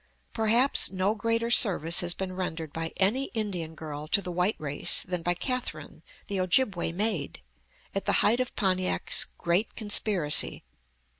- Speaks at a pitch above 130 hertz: Yes, medium, 185 Hz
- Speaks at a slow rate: No, average, 150 wpm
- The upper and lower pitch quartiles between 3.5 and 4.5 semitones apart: Yes, average, 4.2 semitones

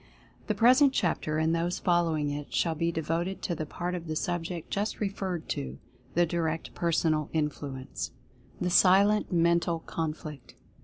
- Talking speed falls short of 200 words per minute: Yes, average, 160 wpm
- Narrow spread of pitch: Yes, narrow, 2.3 semitones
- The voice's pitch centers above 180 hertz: No, medium, 170 Hz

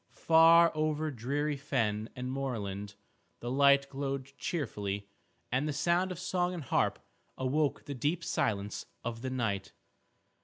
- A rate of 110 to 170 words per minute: Yes, average, 140 wpm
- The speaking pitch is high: No, low, 135 Hz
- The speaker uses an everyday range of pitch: Yes, average, 5.0 semitones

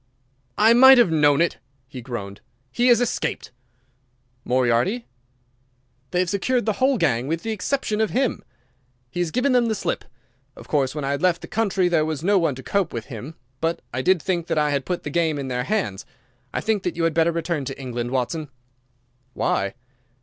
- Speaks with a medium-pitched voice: Yes, medium, 165 Hz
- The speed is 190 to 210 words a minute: Yes, average, 200 wpm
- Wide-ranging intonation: Yes, wide, 7.3 semitones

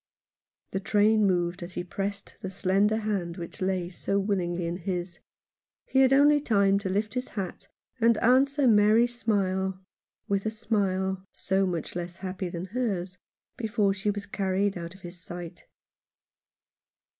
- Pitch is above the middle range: Yes, high, 195 Hz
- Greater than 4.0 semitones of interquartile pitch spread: No, average, 2.8 semitones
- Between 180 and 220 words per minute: No, average, 160 wpm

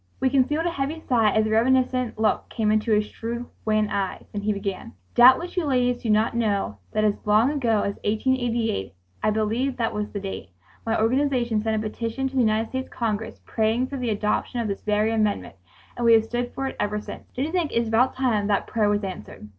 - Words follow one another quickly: Yes, fast, 225 wpm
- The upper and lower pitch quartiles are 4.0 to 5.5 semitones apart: No, average, 3.1 semitones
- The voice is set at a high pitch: Yes, high, 225 Hz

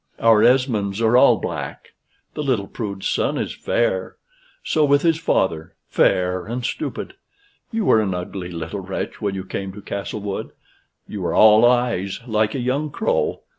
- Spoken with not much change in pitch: No, wide, 5.6 semitones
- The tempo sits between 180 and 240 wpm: No, average, 165 wpm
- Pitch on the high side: No, low, 110 Hz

